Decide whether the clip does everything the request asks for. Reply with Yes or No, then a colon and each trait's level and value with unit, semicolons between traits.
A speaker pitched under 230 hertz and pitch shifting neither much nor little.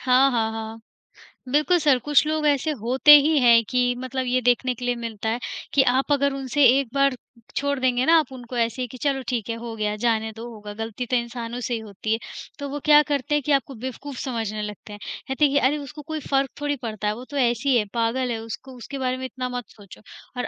No: very high, 250 Hz; average, 3.3 semitones